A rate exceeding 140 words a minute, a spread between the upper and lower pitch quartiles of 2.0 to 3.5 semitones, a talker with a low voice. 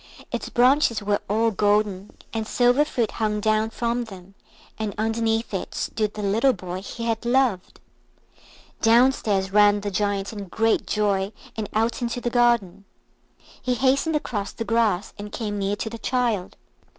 No: average, 160 wpm; narrow, 2.6 semitones; high, 220 Hz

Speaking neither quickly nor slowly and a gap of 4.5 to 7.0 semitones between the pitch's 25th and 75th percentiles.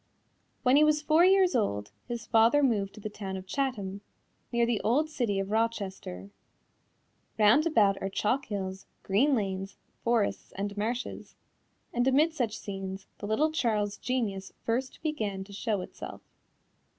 Yes: average, 150 wpm; average, 4.9 semitones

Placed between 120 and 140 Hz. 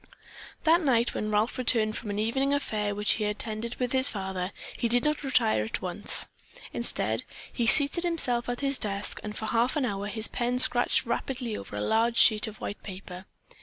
No: high, 230 Hz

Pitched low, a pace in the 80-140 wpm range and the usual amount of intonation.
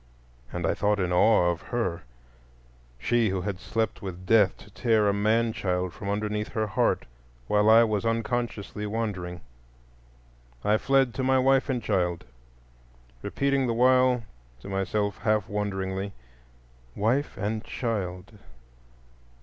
Yes: low, 105 Hz; slow, 135 wpm; average, 3.8 semitones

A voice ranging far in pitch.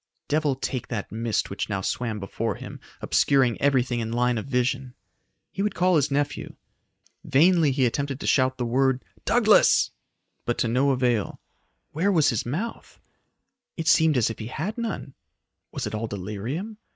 No: average, 4.2 semitones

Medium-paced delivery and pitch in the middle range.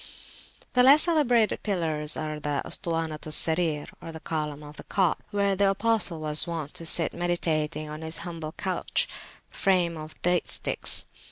Yes: average, 160 wpm; medium, 165 Hz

